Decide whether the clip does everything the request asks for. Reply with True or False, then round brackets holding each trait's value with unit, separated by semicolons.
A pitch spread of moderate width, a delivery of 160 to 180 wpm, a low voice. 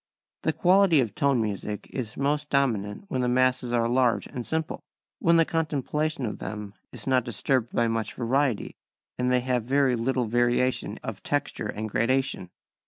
True (3.2 semitones; 165 wpm; 125 Hz)